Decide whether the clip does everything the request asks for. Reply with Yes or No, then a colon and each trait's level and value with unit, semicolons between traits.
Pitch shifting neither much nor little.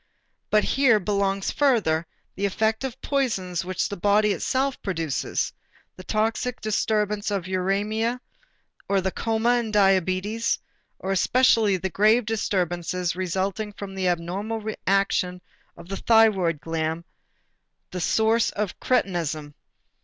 Yes: average, 3.3 semitones